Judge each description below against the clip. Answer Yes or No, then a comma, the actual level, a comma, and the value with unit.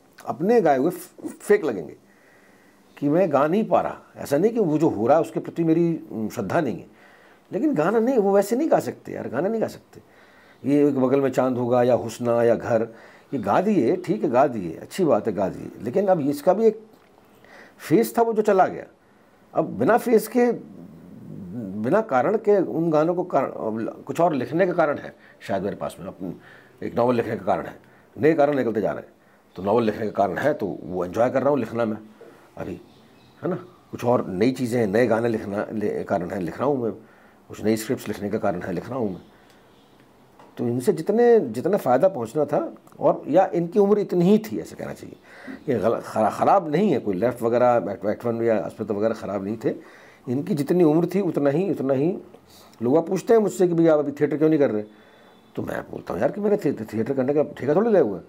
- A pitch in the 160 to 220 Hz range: No, medium, 140 Hz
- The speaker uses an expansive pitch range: Yes, wide, 8.4 semitones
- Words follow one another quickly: Yes, fast, 220 wpm